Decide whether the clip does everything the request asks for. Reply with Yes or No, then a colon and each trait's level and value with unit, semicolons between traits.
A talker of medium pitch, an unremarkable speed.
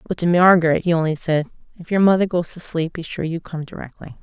No: medium, 170 Hz; fast, 240 wpm